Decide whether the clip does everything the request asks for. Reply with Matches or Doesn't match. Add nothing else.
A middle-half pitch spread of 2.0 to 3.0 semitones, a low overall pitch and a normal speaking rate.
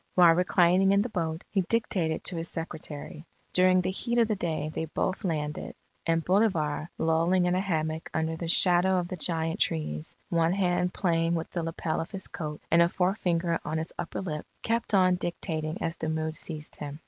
Doesn't match